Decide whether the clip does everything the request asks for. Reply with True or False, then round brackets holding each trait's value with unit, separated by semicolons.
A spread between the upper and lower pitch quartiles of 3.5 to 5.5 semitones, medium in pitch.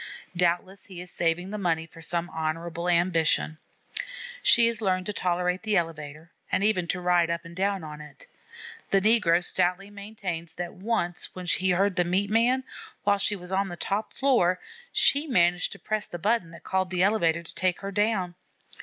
False (2.8 semitones; 180 Hz)